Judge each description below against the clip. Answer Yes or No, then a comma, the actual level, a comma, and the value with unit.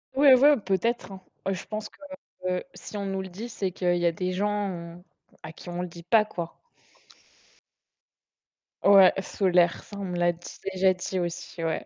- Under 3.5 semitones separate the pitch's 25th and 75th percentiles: Yes, narrow, 2.6 semitones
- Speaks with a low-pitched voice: No, medium, 185 Hz